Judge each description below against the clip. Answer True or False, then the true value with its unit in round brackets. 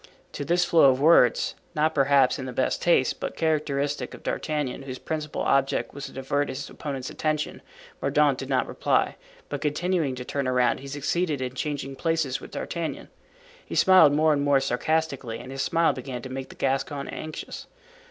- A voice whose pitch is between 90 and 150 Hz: True (140 Hz)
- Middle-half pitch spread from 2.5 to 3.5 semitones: True (2.8 semitones)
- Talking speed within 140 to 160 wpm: False (180 wpm)